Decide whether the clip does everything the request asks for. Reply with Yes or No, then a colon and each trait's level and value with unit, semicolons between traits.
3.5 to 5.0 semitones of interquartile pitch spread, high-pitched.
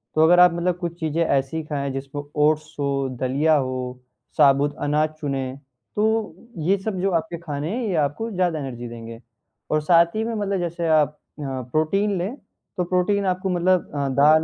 No: average, 4.2 semitones; medium, 160 Hz